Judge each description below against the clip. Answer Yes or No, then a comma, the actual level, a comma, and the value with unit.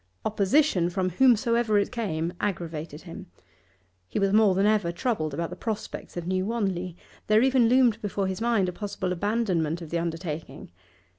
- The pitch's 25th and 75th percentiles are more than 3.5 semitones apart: Yes, average, 4.4 semitones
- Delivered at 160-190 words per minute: Yes, average, 165 wpm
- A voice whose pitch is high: Yes, high, 195 Hz